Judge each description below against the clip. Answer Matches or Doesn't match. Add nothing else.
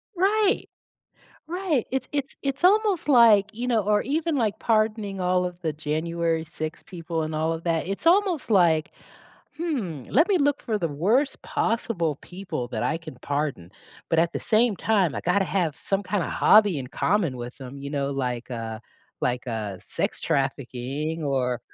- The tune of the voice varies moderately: Doesn't match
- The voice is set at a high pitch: Doesn't match